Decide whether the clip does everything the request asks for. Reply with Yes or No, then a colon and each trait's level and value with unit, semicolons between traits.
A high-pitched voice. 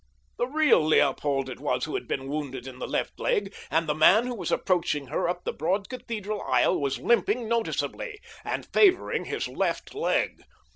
No: medium, 180 Hz